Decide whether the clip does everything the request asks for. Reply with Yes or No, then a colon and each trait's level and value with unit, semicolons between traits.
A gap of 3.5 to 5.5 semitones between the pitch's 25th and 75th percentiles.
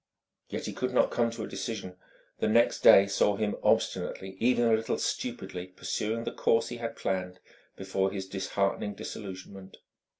No: average, 3.0 semitones